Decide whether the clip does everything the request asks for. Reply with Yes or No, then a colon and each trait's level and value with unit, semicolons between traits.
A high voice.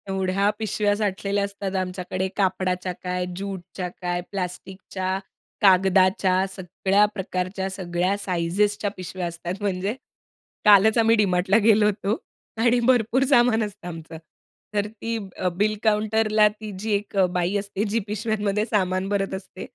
Yes: high, 195 Hz